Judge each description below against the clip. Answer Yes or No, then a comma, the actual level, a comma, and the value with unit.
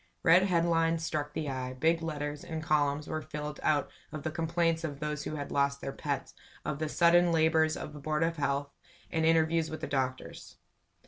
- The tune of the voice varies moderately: No, narrow, 2.0 semitones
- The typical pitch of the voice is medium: Yes, medium, 155 Hz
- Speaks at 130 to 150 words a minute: No, average, 190 wpm